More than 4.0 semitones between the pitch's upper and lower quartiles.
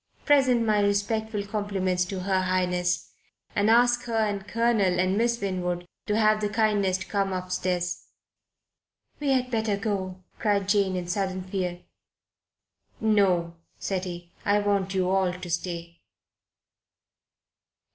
No: average, 2.7 semitones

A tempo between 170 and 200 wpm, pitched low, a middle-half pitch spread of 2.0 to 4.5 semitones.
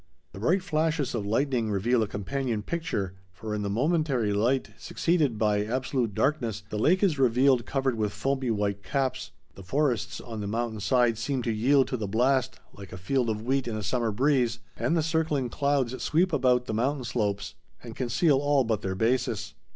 Yes: average, 190 wpm; low, 125 Hz; average, 4.1 semitones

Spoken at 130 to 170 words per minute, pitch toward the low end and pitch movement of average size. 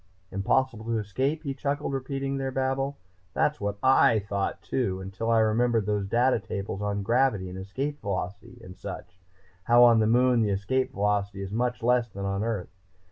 No: average, 180 wpm; low, 115 Hz; average, 4.7 semitones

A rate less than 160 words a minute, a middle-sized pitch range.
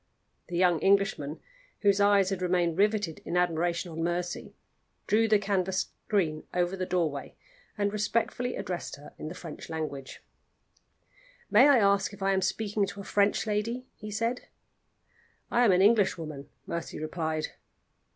Yes: average, 150 wpm; average, 3.6 semitones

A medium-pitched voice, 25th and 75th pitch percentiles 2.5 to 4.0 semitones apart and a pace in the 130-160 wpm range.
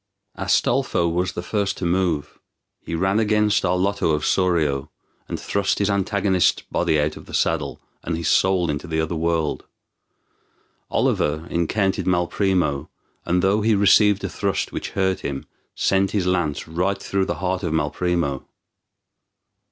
No: very low, 90 Hz; average, 3.1 semitones; average, 150 wpm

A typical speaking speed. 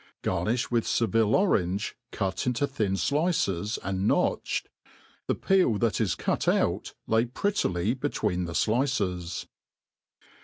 No: slow, 125 wpm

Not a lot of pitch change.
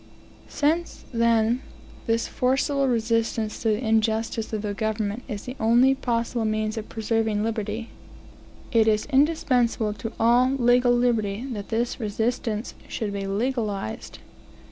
Yes: narrow, 2.1 semitones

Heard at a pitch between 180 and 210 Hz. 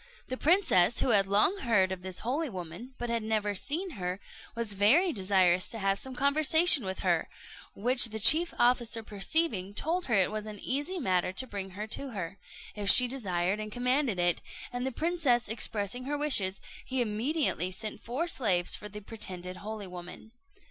No: high, 220 Hz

